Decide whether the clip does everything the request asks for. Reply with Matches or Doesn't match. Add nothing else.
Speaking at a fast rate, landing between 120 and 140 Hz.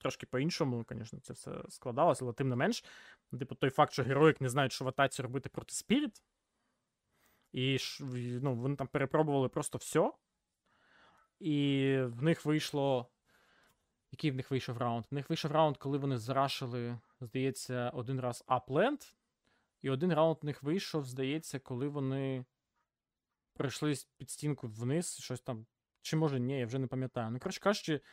Matches